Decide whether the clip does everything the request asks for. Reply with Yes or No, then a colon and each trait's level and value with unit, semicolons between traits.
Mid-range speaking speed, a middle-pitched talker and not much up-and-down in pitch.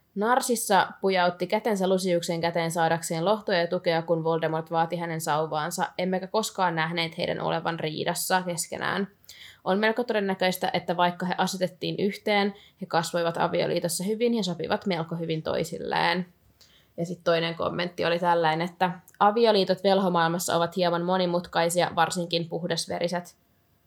Yes: average, 130 wpm; medium, 175 Hz; narrow, 2.0 semitones